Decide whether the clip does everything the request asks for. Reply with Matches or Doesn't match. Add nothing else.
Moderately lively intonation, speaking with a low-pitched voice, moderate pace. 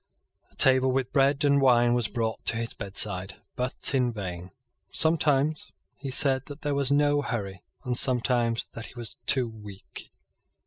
Matches